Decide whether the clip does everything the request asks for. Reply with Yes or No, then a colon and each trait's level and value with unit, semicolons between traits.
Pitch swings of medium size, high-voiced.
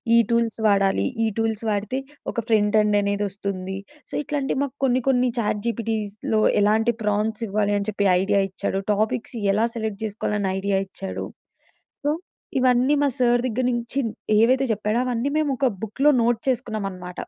Yes: average, 3.1 semitones; high, 220 Hz